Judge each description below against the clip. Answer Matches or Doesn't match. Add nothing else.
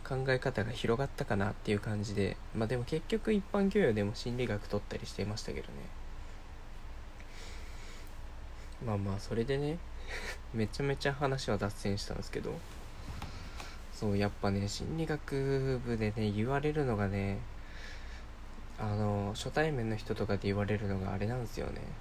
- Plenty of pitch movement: Doesn't match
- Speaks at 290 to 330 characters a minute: Matches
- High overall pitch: Doesn't match